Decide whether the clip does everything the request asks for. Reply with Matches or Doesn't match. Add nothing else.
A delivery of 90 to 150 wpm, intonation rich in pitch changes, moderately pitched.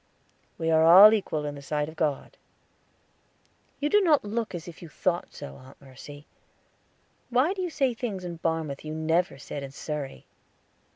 Doesn't match